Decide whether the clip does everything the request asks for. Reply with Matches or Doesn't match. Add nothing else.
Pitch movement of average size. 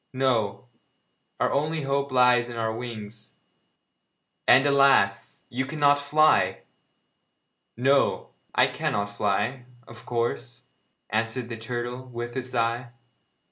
Matches